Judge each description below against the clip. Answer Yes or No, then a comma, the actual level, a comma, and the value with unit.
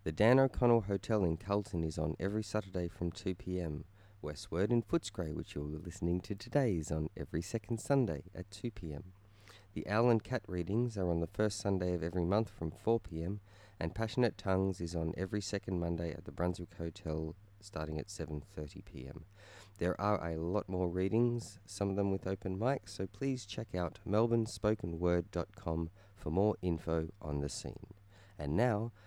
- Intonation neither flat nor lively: Yes, average, 3.8 semitones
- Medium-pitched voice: No, very low, 95 Hz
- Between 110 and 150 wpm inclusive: No, average, 170 wpm